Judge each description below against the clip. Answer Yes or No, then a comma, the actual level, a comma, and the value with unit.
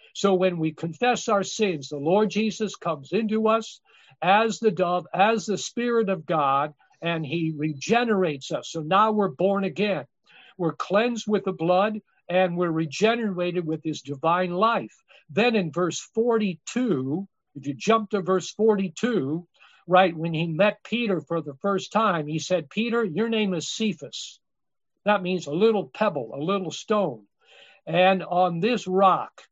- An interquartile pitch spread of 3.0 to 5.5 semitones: Yes, average, 4.3 semitones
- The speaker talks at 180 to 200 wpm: No, average, 160 wpm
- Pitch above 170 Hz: Yes, high, 190 Hz